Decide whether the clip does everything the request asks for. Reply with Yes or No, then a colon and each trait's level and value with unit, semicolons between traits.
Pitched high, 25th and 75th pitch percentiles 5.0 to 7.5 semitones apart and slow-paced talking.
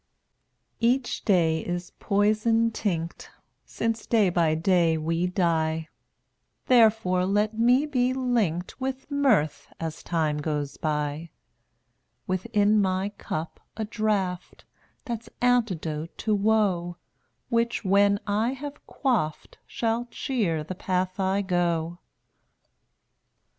Yes: high, 195 Hz; average, 5.3 semitones; slow, 115 wpm